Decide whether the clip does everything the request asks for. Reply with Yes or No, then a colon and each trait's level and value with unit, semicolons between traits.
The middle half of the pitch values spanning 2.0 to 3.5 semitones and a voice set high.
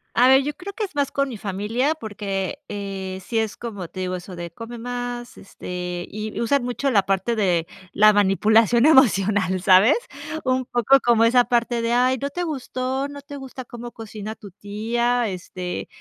No: average, 4.5 semitones; high, 230 Hz